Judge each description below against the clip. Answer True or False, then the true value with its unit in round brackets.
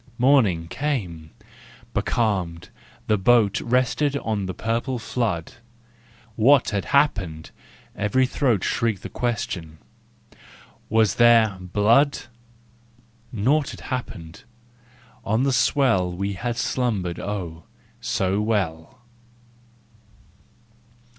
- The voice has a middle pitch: False (110 Hz)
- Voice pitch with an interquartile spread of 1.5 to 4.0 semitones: False (4.9 semitones)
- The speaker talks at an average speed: False (100 wpm)